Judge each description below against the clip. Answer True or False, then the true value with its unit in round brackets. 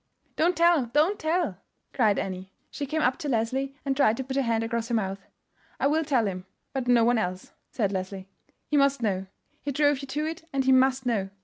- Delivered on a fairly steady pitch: False (4.5 semitones)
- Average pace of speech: False (220 wpm)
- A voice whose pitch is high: True (260 Hz)